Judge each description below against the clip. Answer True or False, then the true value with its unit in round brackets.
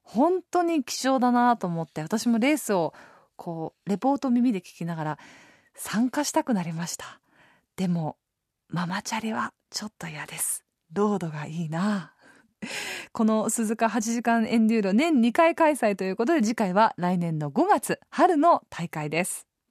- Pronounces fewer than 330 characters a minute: True (295 characters per minute)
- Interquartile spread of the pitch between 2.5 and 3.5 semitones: False (5.9 semitones)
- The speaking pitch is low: False (220 Hz)